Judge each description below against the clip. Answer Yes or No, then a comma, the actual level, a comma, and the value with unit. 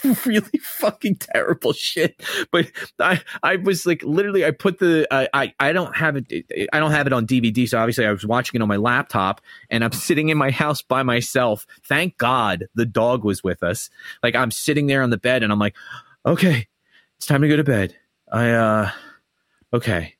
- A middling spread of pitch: No, wide, 5.9 semitones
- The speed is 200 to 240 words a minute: Yes, fast, 205 wpm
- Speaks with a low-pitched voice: Yes, low, 130 Hz